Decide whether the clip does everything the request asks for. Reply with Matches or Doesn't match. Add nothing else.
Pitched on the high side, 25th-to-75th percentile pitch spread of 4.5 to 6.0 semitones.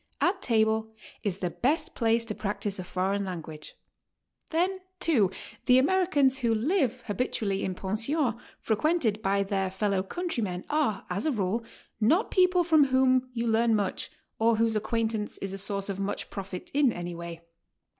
Matches